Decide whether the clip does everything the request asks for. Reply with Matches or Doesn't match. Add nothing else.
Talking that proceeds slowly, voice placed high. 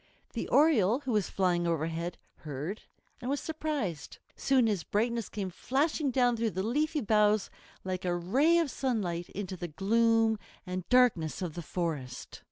Doesn't match